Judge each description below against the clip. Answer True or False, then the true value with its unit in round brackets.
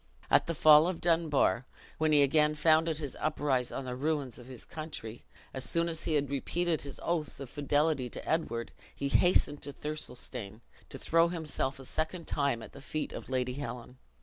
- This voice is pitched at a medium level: True (145 Hz)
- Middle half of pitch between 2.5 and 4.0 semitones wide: True (3.5 semitones)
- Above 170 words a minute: True (190 wpm)